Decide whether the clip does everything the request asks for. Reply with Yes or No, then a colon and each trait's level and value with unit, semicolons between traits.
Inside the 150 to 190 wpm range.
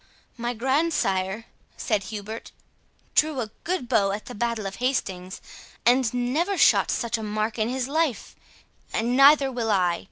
Yes: average, 155 wpm